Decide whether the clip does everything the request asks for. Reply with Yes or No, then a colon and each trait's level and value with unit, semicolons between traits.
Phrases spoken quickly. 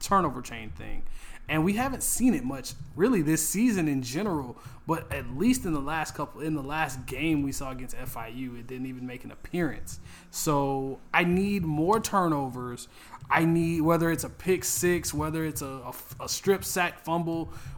No: average, 185 wpm